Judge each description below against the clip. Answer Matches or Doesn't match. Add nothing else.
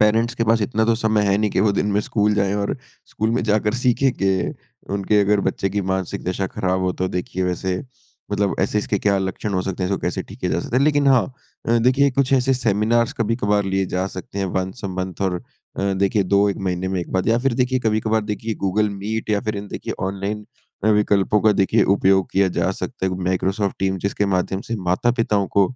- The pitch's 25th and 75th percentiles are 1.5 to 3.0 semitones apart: Matches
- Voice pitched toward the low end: Matches